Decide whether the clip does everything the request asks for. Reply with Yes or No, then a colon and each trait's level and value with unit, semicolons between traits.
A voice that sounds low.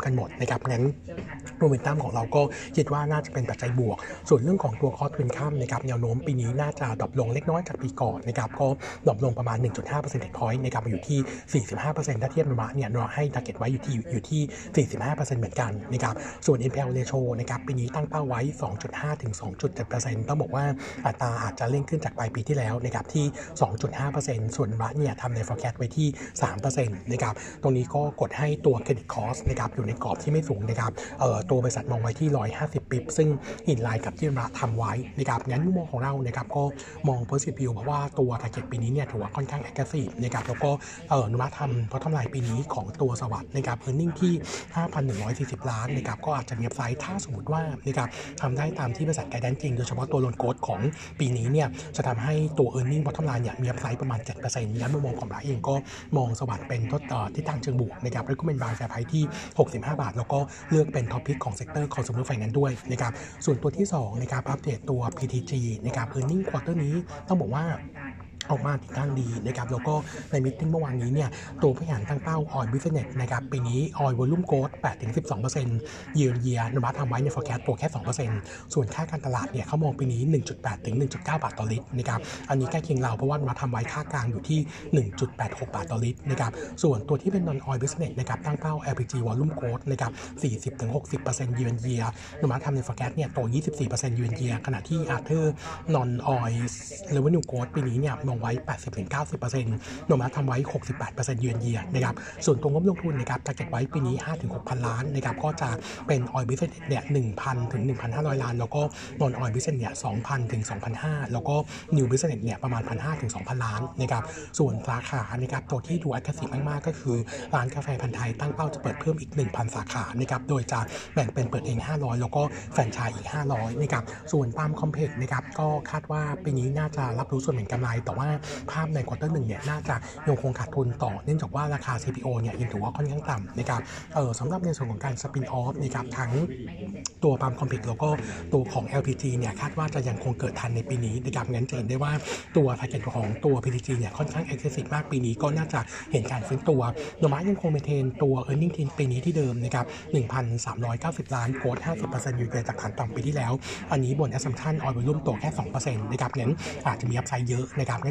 Yes: low, 130 Hz